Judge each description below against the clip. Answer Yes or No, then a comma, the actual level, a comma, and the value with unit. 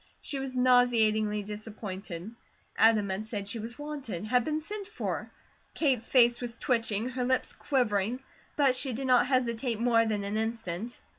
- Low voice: No, high, 235 Hz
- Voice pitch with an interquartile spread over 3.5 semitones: No, average, 3.2 semitones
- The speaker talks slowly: No, average, 160 wpm